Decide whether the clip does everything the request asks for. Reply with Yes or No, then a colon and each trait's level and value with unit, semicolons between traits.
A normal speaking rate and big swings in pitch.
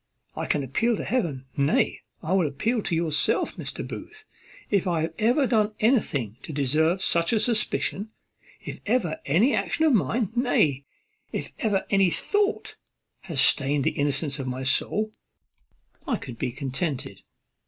Yes: average, 155 wpm; wide, 7.7 semitones